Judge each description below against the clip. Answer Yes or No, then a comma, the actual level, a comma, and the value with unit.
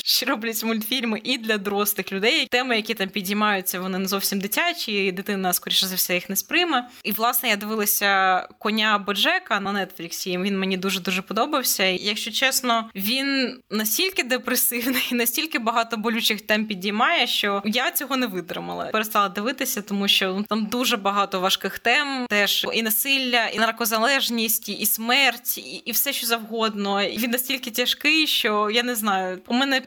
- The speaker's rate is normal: No, fast, 165 wpm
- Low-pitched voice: No, high, 225 Hz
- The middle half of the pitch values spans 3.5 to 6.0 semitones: Yes, average, 3.8 semitones